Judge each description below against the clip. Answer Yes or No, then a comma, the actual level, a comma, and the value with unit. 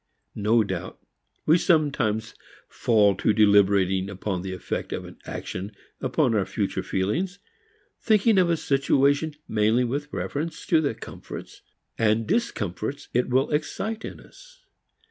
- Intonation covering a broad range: Yes, wide, 7.3 semitones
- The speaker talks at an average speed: No, slow, 130 wpm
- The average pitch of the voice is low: Yes, low, 125 Hz